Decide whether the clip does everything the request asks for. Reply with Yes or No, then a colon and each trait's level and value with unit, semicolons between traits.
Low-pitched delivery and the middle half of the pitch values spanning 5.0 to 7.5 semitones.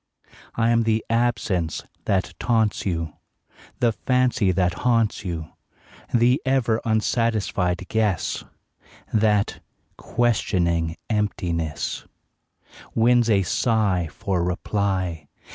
No: low, 105 Hz; average, 4.4 semitones